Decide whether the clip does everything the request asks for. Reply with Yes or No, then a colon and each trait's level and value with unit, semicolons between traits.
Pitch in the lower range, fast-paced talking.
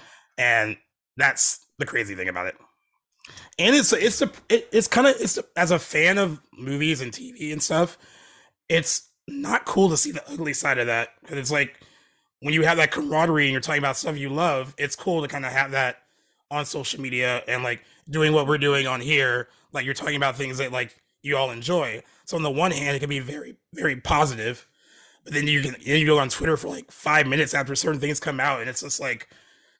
No: medium, 145 Hz; fast, 225 wpm